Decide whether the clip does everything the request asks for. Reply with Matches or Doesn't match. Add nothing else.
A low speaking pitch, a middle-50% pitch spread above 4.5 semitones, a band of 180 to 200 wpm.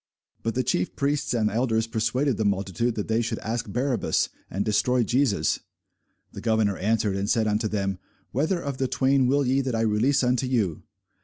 Doesn't match